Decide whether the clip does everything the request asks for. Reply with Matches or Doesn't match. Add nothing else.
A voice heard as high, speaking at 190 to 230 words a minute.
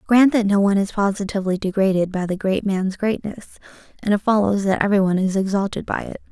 Matches